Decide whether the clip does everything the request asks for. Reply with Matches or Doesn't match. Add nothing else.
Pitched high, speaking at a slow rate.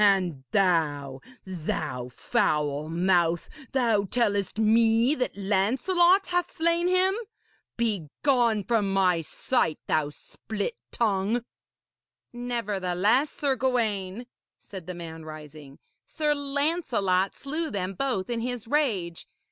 Matches